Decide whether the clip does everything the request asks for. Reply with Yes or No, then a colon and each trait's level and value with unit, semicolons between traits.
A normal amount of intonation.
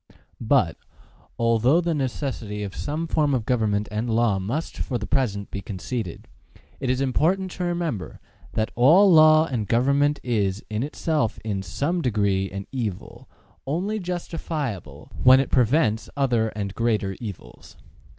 No: wide, 6.3 semitones